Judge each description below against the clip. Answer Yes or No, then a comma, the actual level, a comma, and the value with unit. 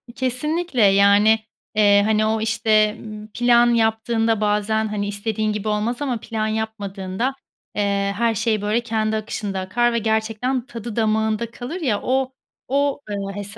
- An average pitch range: No, narrow, 2.1 semitones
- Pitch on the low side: No, high, 220 Hz